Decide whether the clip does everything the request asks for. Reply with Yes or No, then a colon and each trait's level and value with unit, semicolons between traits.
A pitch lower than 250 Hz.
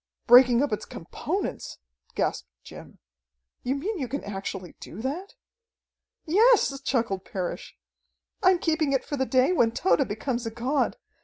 No: very high, 265 Hz